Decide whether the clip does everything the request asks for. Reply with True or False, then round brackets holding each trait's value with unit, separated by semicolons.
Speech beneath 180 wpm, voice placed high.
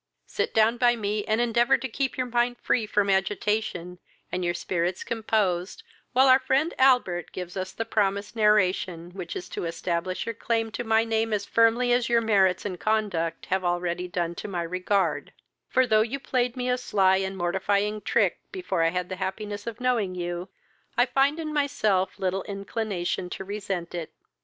False (185 wpm; 205 Hz)